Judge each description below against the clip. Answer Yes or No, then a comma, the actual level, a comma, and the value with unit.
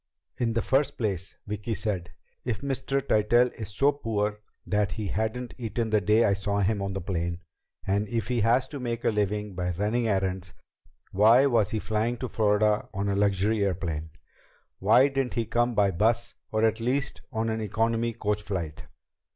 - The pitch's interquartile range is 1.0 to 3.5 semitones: Yes, average, 2.8 semitones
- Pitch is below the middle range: Yes, low, 110 Hz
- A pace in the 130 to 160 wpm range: No, average, 185 wpm